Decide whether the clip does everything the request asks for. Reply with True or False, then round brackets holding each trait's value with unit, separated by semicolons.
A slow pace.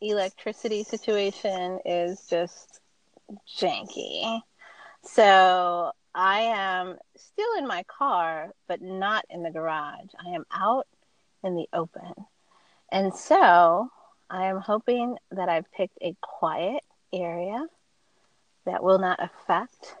True (115 wpm)